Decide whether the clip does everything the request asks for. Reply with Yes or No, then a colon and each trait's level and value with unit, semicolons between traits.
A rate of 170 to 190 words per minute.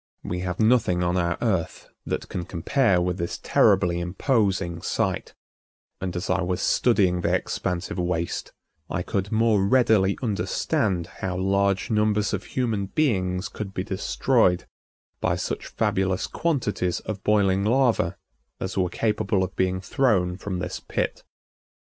No: average, 140 wpm